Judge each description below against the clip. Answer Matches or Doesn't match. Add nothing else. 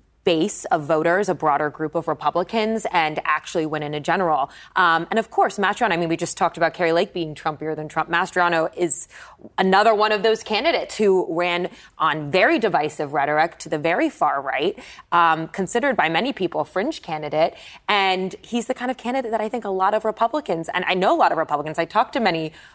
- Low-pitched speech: Doesn't match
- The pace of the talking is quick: Matches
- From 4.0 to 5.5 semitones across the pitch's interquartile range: Matches